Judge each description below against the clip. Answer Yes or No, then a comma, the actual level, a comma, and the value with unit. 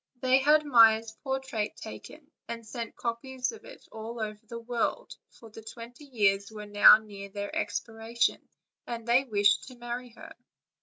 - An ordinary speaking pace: Yes, average, 160 wpm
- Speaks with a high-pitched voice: Yes, high, 230 Hz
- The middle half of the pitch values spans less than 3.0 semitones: Yes, narrow, 2.5 semitones